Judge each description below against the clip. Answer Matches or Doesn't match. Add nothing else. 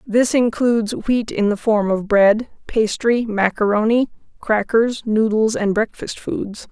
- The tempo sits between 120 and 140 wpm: Matches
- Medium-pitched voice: Doesn't match